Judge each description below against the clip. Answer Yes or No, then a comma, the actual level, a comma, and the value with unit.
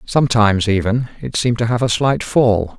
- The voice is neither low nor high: No, low, 115 Hz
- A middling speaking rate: Yes, average, 195 wpm